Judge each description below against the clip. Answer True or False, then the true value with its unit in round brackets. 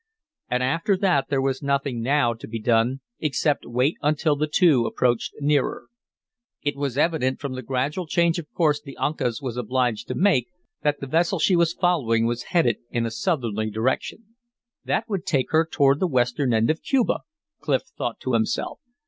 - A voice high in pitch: False (140 Hz)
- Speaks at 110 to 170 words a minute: False (180 wpm)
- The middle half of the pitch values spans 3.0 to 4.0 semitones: False (4.7 semitones)